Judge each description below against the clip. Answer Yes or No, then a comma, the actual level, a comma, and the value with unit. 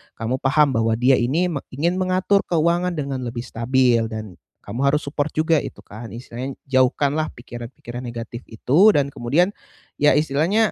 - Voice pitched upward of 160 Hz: No, low, 135 Hz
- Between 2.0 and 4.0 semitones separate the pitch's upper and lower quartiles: No, average, 4.7 semitones